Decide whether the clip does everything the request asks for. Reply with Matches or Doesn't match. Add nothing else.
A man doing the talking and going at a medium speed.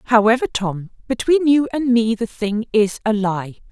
Doesn't match